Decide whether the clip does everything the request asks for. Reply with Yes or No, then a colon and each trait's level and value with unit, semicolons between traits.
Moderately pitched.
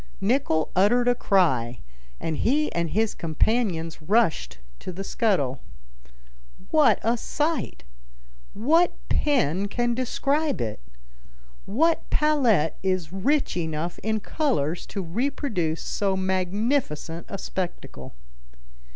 No: high, 200 Hz